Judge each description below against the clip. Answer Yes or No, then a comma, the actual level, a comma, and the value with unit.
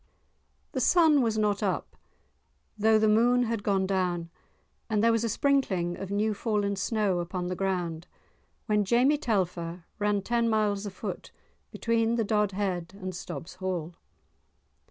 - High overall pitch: Yes, high, 205 Hz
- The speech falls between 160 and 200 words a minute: No, average, 150 wpm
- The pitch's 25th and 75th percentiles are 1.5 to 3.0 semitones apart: No, average, 3.4 semitones